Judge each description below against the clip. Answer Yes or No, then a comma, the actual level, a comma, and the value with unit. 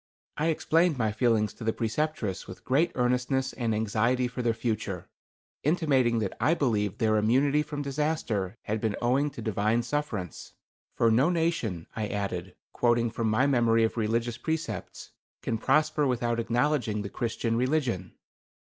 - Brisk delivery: No, average, 155 wpm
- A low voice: Yes, low, 120 Hz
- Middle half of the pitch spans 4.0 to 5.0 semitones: Yes, average, 4.4 semitones